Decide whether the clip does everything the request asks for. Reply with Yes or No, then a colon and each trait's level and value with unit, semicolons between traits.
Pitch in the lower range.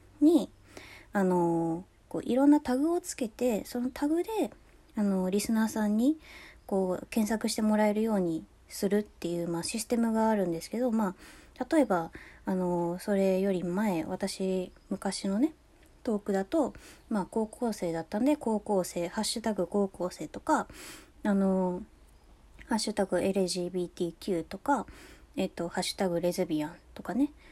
No: high, 200 Hz